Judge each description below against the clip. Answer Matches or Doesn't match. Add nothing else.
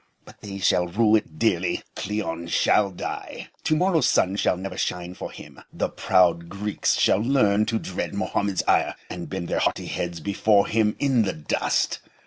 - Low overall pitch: Matches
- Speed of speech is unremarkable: Matches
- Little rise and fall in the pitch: Doesn't match